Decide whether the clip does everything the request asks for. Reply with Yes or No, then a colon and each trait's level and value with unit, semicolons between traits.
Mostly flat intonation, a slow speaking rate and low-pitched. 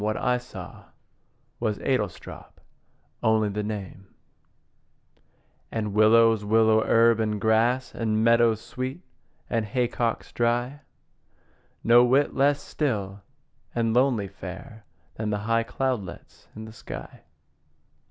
Yes: narrow, 2.2 semitones; slow, 110 wpm; low, 115 Hz